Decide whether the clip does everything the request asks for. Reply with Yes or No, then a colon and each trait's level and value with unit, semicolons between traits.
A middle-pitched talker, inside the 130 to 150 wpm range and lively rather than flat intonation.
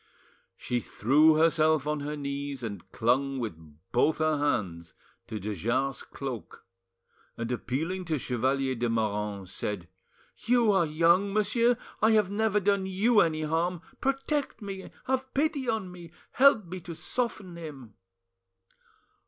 Yes: medium, 155 Hz; average, 140 wpm; wide, 8.2 semitones